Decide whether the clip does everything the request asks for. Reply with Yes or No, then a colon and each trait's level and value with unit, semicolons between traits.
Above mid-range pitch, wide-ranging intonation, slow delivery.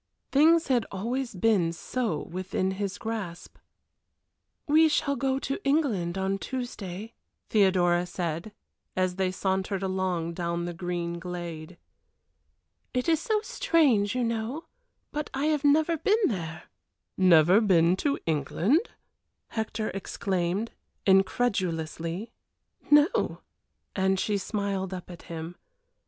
Yes: high, 195 Hz; wide, 6.2 semitones; slow, 115 wpm